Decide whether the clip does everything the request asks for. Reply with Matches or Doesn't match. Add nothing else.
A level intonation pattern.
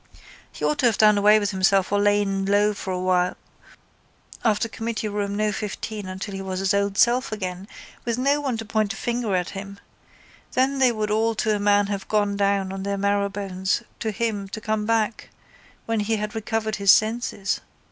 Matches